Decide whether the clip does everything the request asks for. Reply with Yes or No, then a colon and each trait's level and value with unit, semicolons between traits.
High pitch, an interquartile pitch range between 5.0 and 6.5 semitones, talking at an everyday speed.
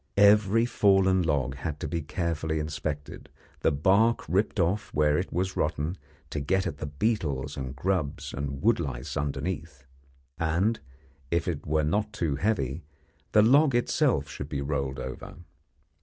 No: very low, 80 Hz; wide, 5.4 semitones; average, 155 wpm